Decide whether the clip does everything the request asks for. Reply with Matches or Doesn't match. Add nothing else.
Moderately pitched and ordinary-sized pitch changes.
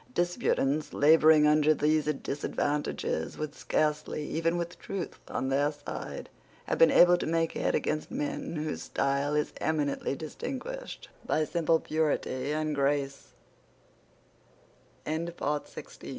Doesn't match